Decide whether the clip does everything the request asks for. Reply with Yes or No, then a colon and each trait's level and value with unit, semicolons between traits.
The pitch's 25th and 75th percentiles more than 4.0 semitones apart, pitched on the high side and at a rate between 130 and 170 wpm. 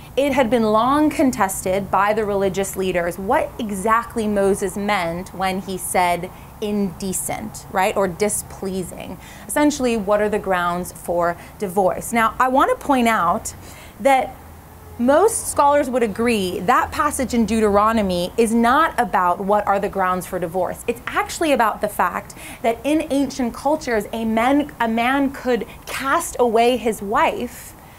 Yes: average, 4.5 semitones; high, 220 Hz; average, 150 wpm